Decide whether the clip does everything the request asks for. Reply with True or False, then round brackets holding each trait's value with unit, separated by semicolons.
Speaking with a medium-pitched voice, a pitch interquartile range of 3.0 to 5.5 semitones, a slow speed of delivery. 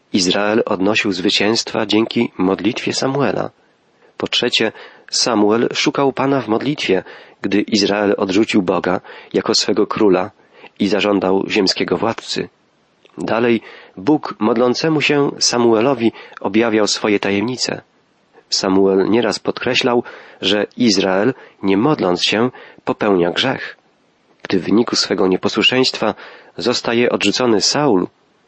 False (110 Hz; 3.4 semitones; 105 wpm)